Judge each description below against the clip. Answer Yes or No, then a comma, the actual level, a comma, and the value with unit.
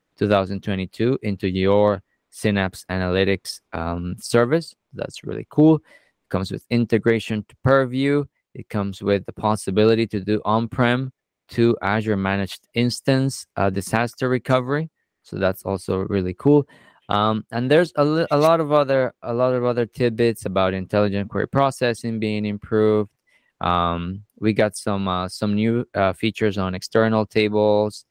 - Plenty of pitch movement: No, average, 3.7 semitones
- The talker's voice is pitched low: Yes, low, 110 Hz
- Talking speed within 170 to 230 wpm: No, average, 145 wpm